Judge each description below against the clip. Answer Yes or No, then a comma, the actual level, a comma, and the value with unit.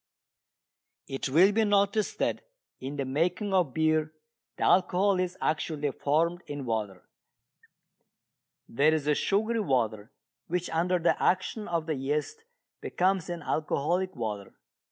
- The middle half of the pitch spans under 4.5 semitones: No, average, 4.8 semitones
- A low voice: No, medium, 160 Hz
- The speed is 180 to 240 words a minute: No, slow, 135 wpm